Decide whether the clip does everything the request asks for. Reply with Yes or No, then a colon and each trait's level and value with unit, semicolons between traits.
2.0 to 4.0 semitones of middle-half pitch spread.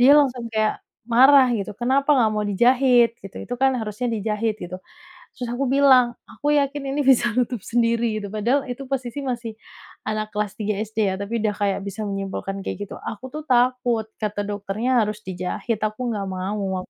Yes: average, 3.4 semitones